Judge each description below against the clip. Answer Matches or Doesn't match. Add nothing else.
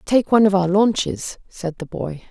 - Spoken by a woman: Matches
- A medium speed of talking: Doesn't match